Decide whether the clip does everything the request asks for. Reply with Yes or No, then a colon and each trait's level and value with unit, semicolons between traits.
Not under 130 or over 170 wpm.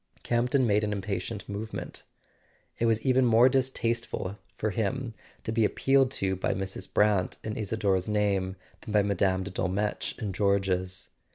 Yes: average, 155 wpm